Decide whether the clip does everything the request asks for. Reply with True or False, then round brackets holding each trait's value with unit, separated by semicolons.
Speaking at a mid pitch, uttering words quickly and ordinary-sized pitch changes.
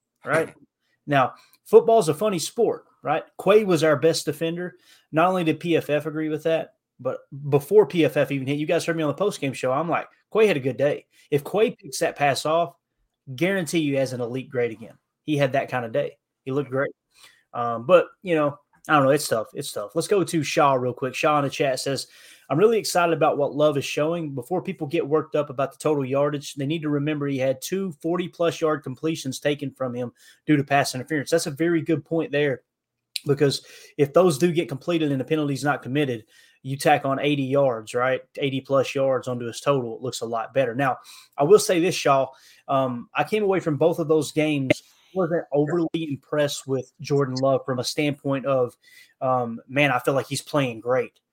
True (145 Hz; 215 wpm; 3.4 semitones)